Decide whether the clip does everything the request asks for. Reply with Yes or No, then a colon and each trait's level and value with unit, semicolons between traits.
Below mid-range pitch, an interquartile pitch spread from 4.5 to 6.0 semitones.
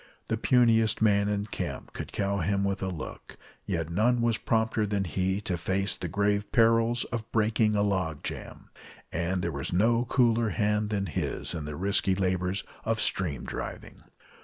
No: low, 100 Hz; average, 3.2 semitones